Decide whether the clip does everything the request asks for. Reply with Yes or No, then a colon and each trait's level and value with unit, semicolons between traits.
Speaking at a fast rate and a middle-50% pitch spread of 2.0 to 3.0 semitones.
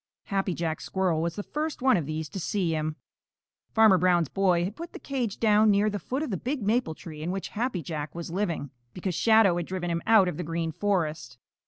No: fast, 225 wpm; average, 4.3 semitones